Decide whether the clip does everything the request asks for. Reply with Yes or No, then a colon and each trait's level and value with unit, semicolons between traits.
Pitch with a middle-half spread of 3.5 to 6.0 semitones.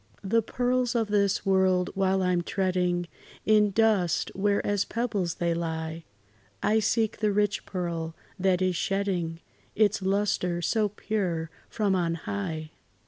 No: average, 3.0 semitones